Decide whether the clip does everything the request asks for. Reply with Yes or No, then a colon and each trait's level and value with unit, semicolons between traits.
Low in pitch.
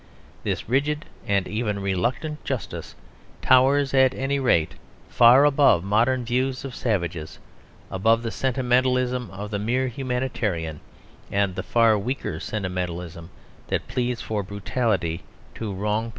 Yes: low, 115 Hz